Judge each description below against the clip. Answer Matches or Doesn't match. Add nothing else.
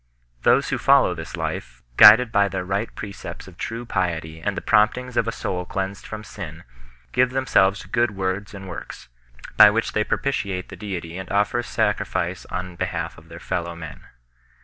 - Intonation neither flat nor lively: Matches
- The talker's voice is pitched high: Doesn't match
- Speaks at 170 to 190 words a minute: Matches